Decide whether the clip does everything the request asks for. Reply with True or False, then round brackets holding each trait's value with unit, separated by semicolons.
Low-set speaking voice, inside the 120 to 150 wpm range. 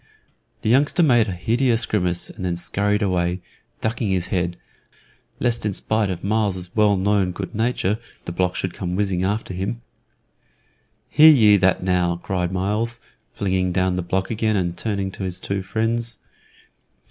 False (100 Hz; 160 wpm)